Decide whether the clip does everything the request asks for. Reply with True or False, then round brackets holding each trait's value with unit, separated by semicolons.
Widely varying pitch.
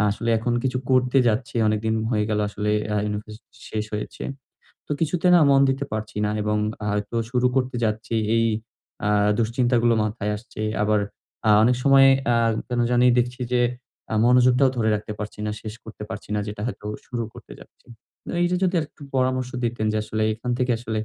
False (2.9 semitones)